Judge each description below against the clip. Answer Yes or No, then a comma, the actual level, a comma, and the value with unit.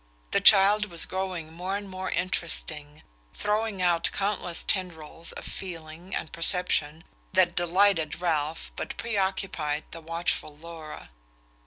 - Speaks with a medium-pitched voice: Yes, medium, 175 Hz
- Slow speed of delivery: Yes, slow, 125 wpm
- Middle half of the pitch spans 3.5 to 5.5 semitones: No, average, 3.0 semitones